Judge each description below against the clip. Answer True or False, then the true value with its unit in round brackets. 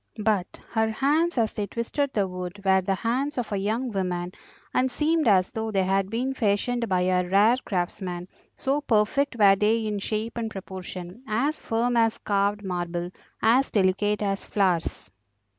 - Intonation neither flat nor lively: True (3.7 semitones)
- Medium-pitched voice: False (210 Hz)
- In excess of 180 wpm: False (170 wpm)